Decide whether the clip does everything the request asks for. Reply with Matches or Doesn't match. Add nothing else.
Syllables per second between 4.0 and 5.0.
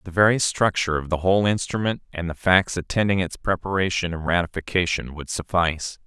Doesn't match